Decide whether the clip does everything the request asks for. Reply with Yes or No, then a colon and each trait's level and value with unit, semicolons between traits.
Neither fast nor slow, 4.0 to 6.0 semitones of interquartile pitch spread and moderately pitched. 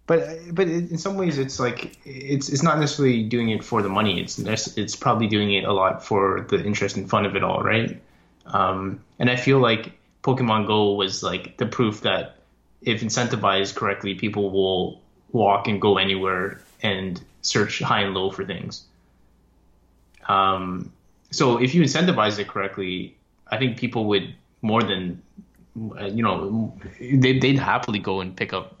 No: average, 170 wpm; average, 4.6 semitones; low, 105 Hz